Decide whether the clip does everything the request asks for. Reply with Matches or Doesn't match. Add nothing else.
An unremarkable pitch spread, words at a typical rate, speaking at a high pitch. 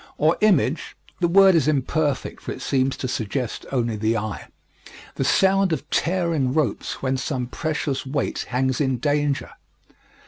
Doesn't match